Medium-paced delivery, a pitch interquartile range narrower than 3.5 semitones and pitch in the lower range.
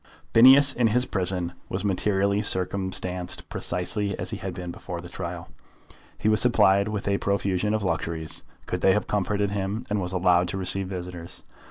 Yes: average, 175 wpm; narrow, 2.5 semitones; very low, 95 Hz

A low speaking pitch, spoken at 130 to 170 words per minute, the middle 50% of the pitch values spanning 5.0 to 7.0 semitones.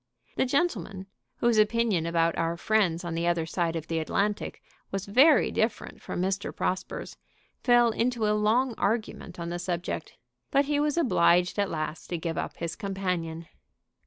No: high, 190 Hz; average, 165 wpm; average, 5.3 semitones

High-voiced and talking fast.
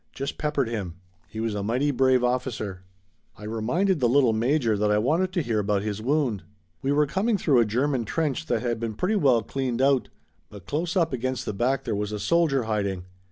No: low, 125 Hz; fast, 210 wpm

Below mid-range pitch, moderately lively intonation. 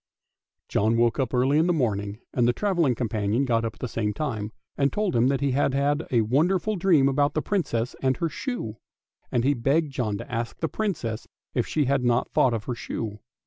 Yes: low, 130 Hz; average, 4.6 semitones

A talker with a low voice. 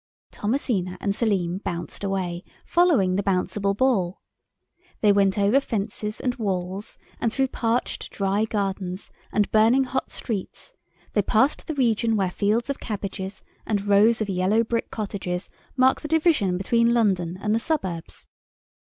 No: high, 205 Hz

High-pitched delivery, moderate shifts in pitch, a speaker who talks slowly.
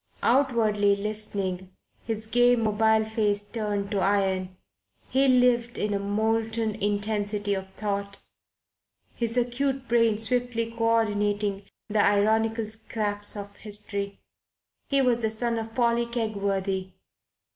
No: high, 215 Hz; narrow, 2.2 semitones; slow, 115 wpm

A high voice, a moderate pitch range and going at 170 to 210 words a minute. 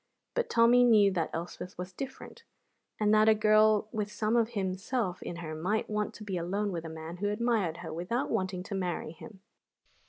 Yes: high, 205 Hz; average, 3.4 semitones; average, 195 wpm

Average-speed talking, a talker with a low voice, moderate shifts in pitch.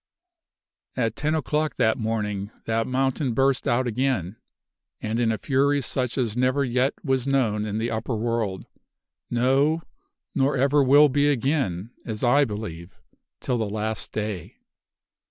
Yes: average, 145 wpm; low, 120 Hz; average, 3.8 semitones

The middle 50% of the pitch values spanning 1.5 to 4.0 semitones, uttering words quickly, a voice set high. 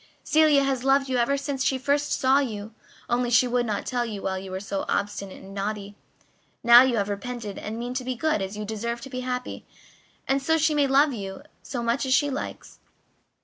No: average, 4.4 semitones; fast, 215 wpm; high, 245 Hz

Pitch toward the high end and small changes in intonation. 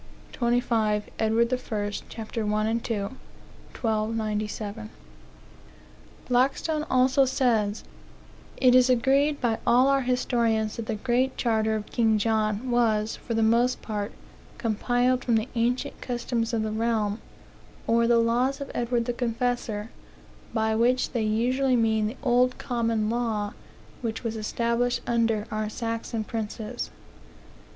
Yes: high, 230 Hz; narrow, 2.1 semitones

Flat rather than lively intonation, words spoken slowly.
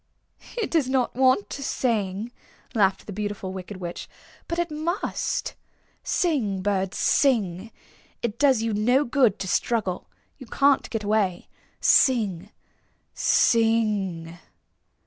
No: average, 5.3 semitones; slow, 120 wpm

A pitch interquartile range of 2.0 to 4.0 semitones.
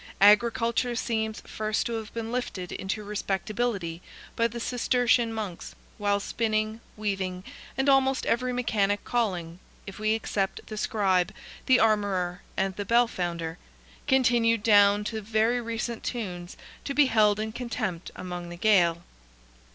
Yes: average, 3.3 semitones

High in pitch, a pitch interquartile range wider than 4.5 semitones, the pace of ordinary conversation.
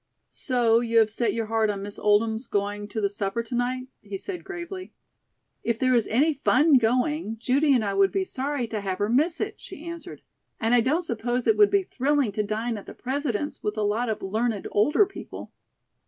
No: high, 235 Hz; average, 5.1 semitones; fast, 215 wpm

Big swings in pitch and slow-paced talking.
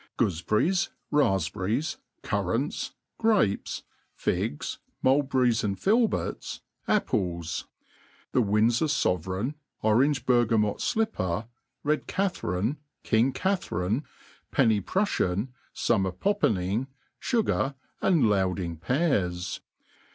Yes: wide, 7.8 semitones; slow, 80 wpm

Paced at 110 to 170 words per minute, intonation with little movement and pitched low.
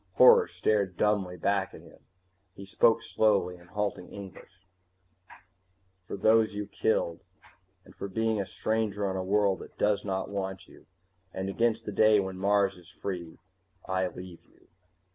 Yes: average, 160 wpm; narrow, 2.1 semitones; low, 100 Hz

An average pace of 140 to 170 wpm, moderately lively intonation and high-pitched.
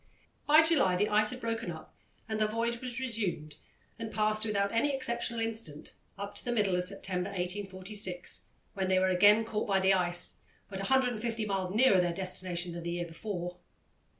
No: average, 180 wpm; average, 3.8 semitones; high, 200 Hz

